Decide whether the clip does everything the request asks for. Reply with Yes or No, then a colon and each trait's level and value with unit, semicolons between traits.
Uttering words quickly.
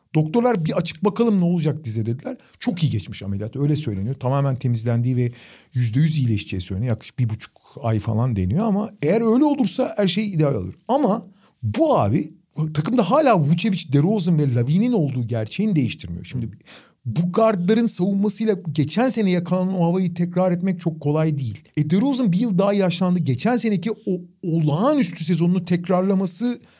Yes: fast, 165 wpm